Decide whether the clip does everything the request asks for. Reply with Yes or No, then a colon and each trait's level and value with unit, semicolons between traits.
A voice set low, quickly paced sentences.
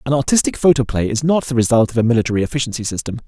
Yes: low, 125 Hz; fast, 220 wpm